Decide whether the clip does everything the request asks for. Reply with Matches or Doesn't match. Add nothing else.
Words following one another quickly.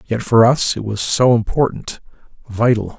Doesn't match